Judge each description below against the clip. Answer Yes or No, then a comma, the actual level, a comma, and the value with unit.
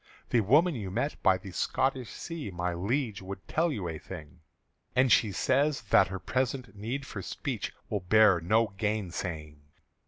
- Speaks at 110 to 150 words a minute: No, average, 165 wpm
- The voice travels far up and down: Yes, wide, 5.9 semitones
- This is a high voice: No, low, 105 Hz